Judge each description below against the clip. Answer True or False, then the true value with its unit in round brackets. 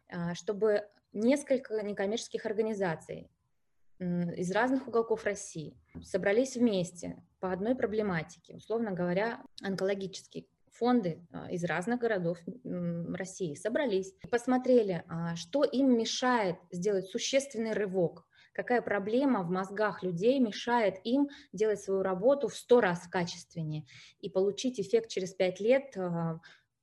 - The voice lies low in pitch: False (200 Hz)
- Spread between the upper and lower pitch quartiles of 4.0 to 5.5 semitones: True (4.7 semitones)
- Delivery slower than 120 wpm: True (110 wpm)